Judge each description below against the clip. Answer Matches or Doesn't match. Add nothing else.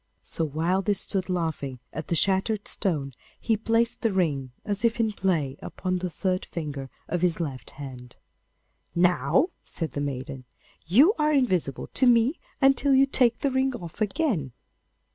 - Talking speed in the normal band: Matches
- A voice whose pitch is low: Doesn't match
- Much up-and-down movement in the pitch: Matches